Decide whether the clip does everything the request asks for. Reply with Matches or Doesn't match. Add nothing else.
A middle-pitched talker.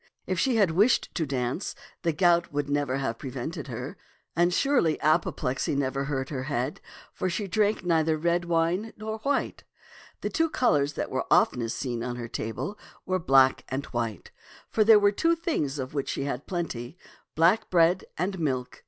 Matches